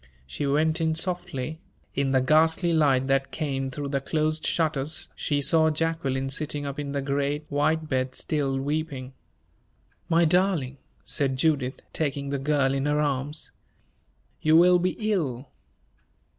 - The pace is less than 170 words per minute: Yes, average, 145 wpm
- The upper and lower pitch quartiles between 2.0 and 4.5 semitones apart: Yes, average, 2.8 semitones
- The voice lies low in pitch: No, medium, 145 Hz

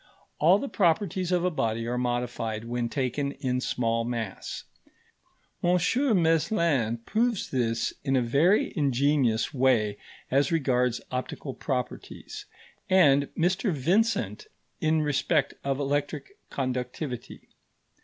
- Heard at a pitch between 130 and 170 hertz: Yes, medium, 140 Hz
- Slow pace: Yes, slow, 115 wpm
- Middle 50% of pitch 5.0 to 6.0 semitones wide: Yes, wide, 5.6 semitones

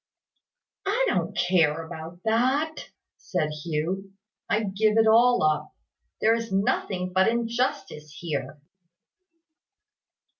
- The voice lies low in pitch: No, high, 195 Hz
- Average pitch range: No, wide, 5.8 semitones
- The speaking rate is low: Yes, slow, 105 wpm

